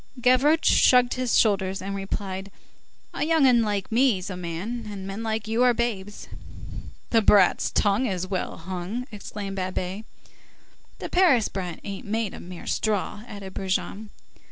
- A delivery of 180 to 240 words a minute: No, average, 145 wpm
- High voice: Yes, high, 205 Hz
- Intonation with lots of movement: No, average, 3.7 semitones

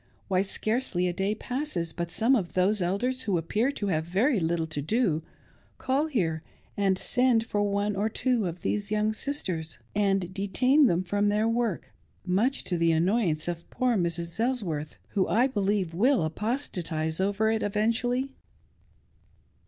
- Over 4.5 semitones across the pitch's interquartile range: Yes, average, 5.1 semitones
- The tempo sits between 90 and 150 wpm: No, average, 160 wpm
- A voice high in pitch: Yes, high, 205 Hz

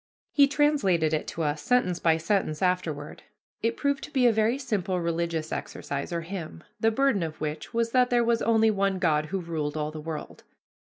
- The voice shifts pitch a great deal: Yes, wide, 6.5 semitones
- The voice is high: No, medium, 180 Hz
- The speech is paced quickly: No, average, 195 wpm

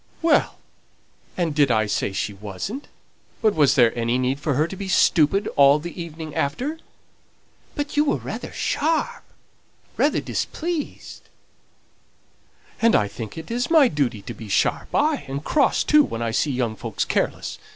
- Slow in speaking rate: No, average, 160 wpm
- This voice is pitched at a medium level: Yes, medium, 150 Hz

